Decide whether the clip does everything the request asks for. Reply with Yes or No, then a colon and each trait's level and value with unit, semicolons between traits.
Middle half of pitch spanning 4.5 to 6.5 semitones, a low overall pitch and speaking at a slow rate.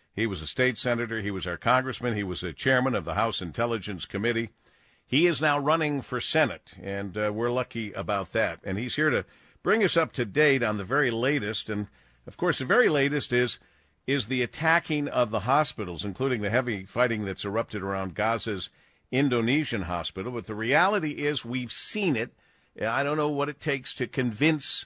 No: average, 5.2 semitones; low, 120 Hz; average, 195 wpm